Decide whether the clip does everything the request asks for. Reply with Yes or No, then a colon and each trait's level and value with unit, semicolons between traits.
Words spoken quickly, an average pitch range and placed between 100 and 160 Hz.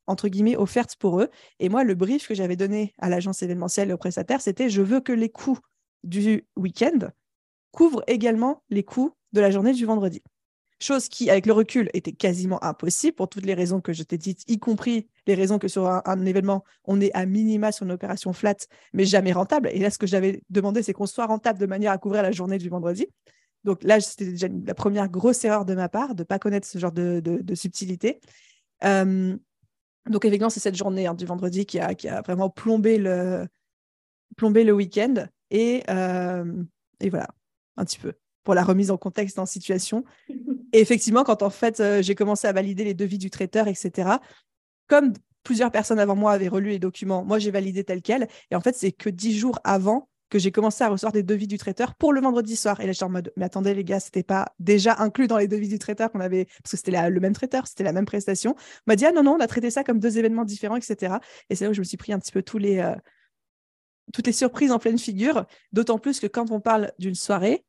No: fast, 240 wpm; average, 3.0 semitones; high, 205 Hz